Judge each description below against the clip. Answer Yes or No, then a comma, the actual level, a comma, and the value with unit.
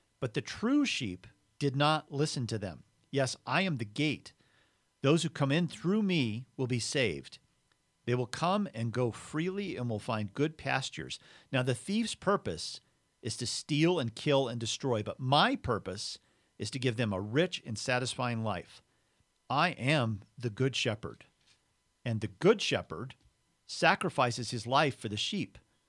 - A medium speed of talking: Yes, average, 165 wpm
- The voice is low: Yes, low, 125 Hz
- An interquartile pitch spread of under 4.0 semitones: No, average, 5.0 semitones